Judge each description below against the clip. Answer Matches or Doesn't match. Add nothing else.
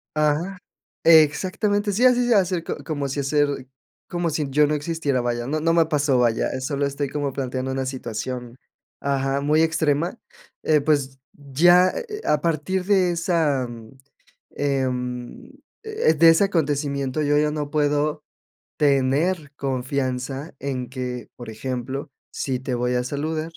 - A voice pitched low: Doesn't match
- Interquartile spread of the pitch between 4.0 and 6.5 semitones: Doesn't match